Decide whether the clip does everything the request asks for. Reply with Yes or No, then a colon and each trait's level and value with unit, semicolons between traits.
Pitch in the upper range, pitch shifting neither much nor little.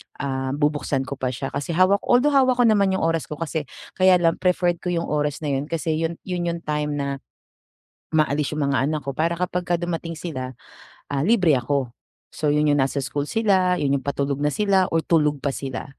No: medium, 155 Hz; average, 3.9 semitones